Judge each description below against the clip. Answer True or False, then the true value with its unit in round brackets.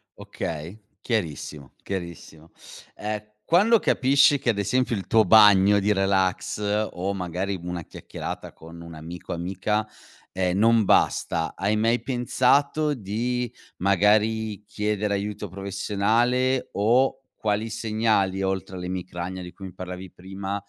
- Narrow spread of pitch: False (3.1 semitones)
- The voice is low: True (100 Hz)